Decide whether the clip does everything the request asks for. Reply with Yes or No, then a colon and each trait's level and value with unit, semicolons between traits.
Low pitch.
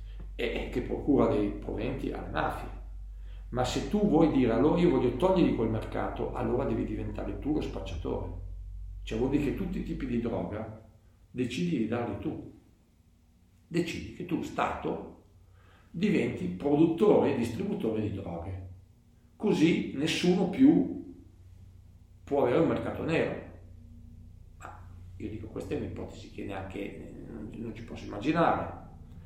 Yes: low, 100 Hz